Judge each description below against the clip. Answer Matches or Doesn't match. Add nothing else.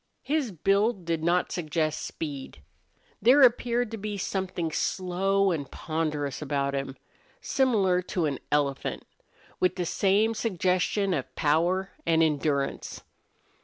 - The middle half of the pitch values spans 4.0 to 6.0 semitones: Matches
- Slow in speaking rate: Matches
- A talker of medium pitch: Matches